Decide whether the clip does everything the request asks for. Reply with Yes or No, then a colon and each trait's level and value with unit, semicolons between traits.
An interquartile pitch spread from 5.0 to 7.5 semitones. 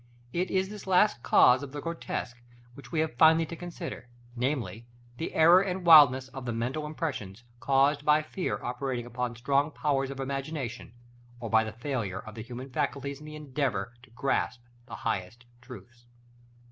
No: average, 4.1 semitones